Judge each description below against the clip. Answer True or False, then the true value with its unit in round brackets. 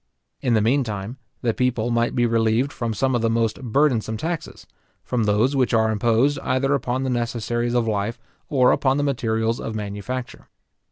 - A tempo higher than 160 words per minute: True (175 wpm)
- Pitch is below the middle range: True (120 Hz)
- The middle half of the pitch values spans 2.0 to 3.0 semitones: True (2.6 semitones)